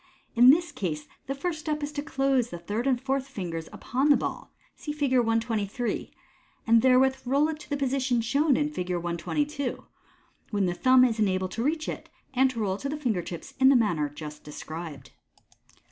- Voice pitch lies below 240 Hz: No, very high, 250 Hz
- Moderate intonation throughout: No, wide, 6.5 semitones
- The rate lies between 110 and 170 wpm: No, average, 200 wpm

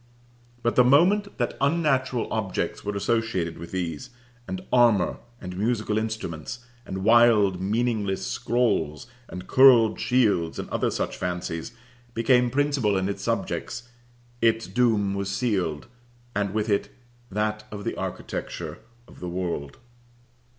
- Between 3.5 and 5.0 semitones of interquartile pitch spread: Yes, average, 4.4 semitones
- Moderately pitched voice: No, low, 110 Hz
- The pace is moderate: No, slow, 130 wpm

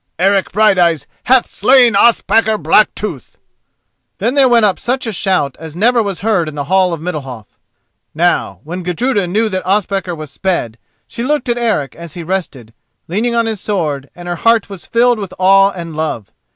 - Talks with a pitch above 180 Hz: Yes, high, 190 Hz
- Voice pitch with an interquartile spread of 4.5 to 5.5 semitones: Yes, average, 5.1 semitones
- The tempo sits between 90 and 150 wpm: No, average, 180 wpm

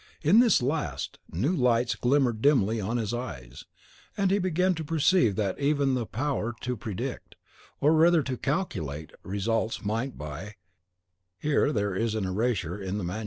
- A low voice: Yes, low, 120 Hz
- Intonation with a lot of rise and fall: Yes, wide, 6.2 semitones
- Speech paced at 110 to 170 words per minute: Yes, average, 165 wpm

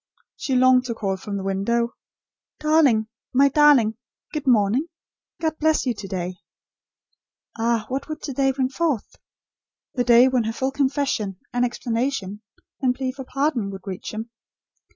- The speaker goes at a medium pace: Yes, average, 155 wpm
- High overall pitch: Yes, very high, 250 Hz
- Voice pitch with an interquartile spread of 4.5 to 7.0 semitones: No, average, 4.1 semitones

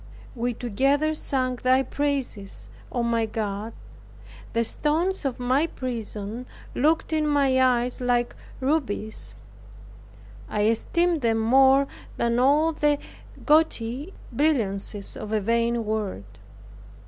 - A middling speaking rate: No, slow, 110 wpm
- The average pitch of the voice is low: No, very high, 250 Hz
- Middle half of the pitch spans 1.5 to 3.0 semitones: No, average, 4.2 semitones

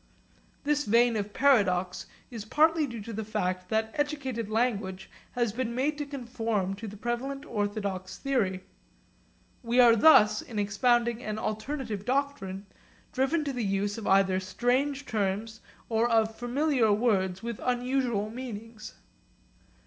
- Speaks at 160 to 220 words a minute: No, average, 140 wpm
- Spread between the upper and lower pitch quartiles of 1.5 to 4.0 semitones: Yes, average, 3.7 semitones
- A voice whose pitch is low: No, high, 225 Hz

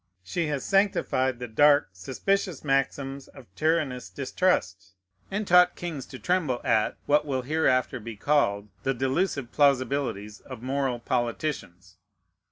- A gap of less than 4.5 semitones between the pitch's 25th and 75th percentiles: Yes, average, 4.1 semitones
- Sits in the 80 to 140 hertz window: Yes, low, 135 Hz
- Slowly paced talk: Yes, slow, 130 wpm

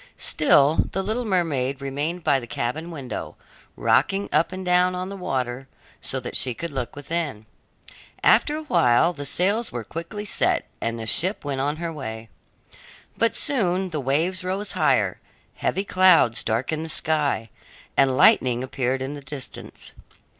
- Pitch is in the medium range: Yes, medium, 150 Hz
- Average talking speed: Yes, average, 160 wpm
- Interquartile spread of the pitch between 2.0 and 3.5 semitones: No, wide, 5.6 semitones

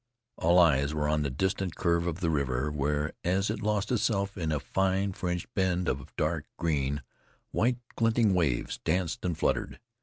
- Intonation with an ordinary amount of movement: Yes, average, 4.4 semitones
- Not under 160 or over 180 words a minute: Yes, average, 175 wpm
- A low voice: Yes, very low, 85 Hz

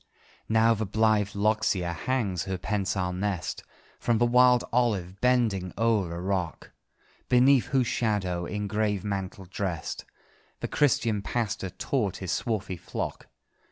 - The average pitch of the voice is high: No, low, 105 Hz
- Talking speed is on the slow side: Yes, slow, 130 wpm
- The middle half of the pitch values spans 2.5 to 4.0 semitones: Yes, average, 3.5 semitones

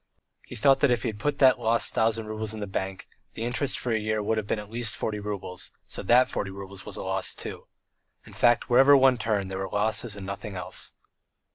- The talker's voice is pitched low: Yes, low, 110 Hz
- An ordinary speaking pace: No, fast, 235 wpm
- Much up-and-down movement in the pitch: No, average, 3.1 semitones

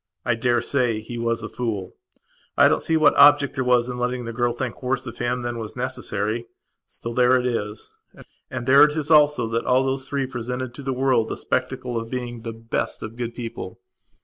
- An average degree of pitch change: No, narrow, 1.9 semitones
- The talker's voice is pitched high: No, low, 125 Hz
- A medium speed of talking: No, fast, 210 wpm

